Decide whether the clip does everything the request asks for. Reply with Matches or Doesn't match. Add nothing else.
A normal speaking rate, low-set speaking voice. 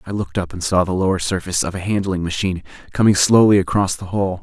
Doesn't match